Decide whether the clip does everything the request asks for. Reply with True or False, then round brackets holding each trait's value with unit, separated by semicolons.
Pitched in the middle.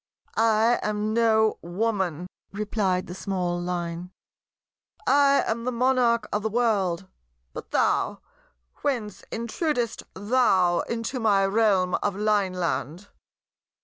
False (210 Hz)